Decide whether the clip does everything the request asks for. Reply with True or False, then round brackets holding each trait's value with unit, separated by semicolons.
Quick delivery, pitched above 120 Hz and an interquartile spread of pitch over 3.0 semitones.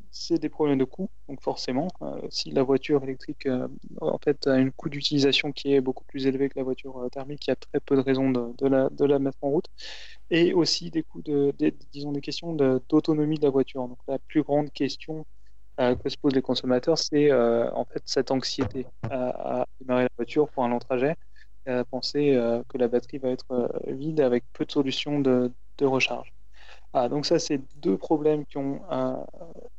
False (225 wpm; 135 Hz; 2.4 semitones)